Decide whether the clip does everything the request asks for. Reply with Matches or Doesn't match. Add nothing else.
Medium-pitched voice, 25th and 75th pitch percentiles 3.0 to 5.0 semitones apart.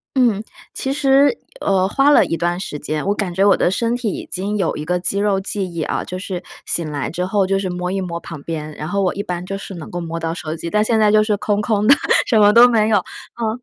Doesn't match